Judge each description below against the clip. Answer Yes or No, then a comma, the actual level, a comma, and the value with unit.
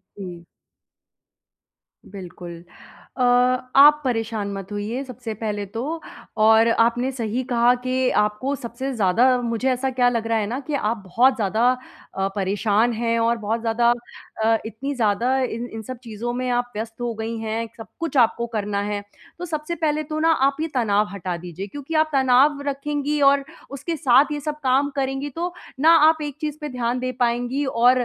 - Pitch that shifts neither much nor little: Yes, average, 3.7 semitones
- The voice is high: Yes, high, 240 Hz